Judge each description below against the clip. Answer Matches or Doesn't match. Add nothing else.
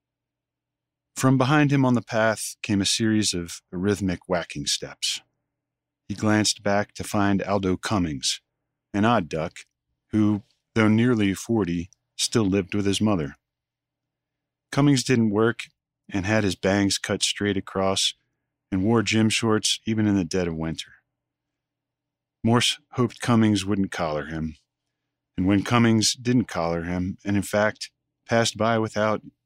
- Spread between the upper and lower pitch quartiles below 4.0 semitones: Matches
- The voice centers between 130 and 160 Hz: Doesn't match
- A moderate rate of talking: Matches